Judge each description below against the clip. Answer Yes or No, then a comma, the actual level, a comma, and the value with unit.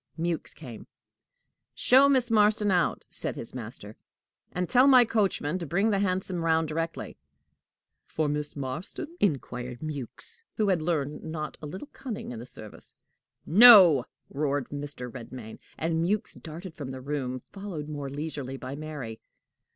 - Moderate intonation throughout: No, wide, 5.7 semitones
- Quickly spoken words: No, average, 150 wpm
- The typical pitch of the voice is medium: Yes, medium, 155 Hz